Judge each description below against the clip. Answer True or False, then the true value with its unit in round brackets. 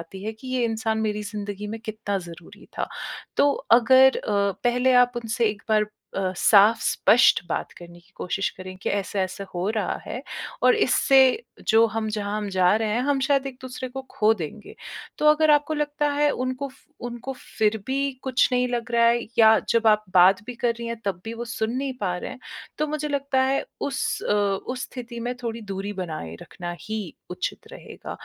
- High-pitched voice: True (225 Hz)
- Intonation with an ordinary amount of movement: True (4.2 semitones)